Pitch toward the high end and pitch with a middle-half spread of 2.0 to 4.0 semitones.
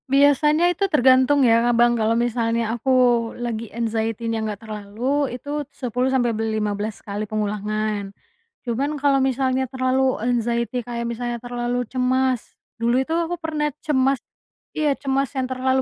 Yes: high, 245 Hz; average, 2.7 semitones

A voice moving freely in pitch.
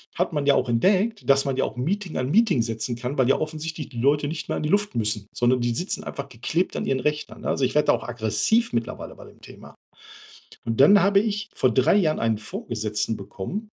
Yes: wide, 7.2 semitones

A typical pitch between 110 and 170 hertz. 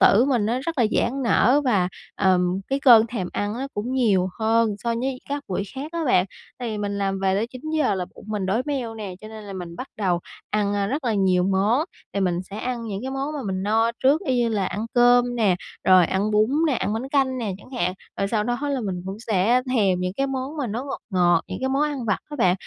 No: high, 220 Hz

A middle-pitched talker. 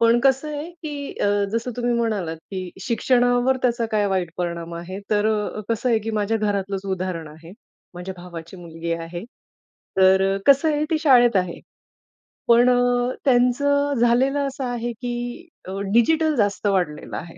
No: high, 230 Hz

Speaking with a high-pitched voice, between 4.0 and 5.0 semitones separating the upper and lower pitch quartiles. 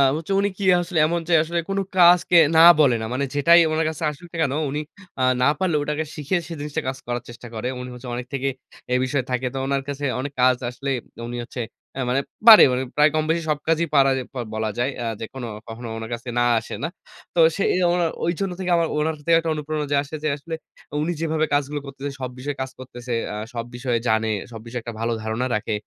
No: medium, 140 Hz; average, 4.5 semitones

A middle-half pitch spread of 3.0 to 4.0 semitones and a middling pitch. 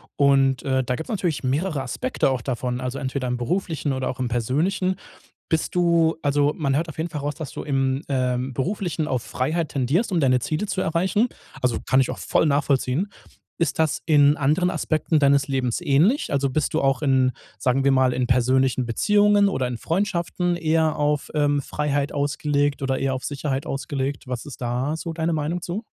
Yes: average, 3.5 semitones; medium, 145 Hz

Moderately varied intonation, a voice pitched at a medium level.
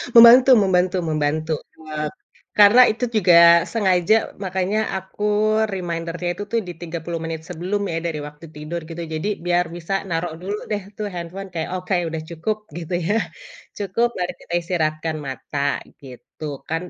Yes: average, 3.4 semitones; medium, 175 Hz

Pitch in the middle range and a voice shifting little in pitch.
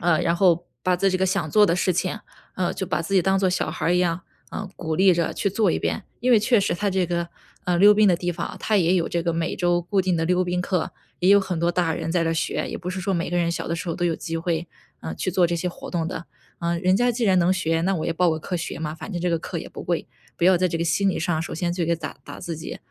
Yes: medium, 175 Hz; narrow, 2.0 semitones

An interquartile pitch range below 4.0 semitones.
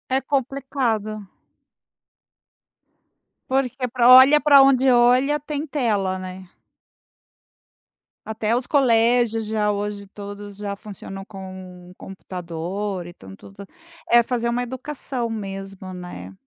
No: average, 4.6 semitones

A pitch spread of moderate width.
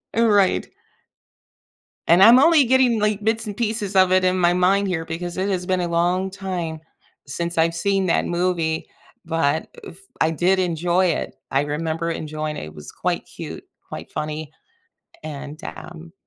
Yes: average, 3.1 semitones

